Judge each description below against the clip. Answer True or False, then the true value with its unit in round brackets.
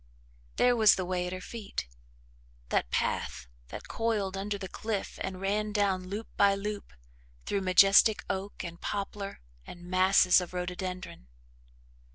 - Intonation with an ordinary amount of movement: False (2.0 semitones)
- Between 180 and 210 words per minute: False (145 wpm)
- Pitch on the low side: False (195 Hz)